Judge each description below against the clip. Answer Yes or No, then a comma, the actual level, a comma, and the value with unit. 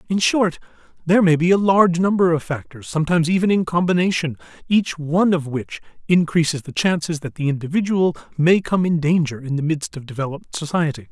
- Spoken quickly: No, average, 185 wpm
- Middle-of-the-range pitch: Yes, medium, 165 Hz